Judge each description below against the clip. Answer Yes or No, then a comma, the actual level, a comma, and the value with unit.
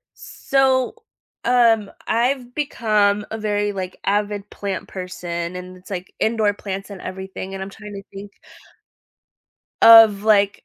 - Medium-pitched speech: No, high, 205 Hz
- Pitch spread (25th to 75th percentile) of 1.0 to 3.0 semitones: Yes, narrow, 2.6 semitones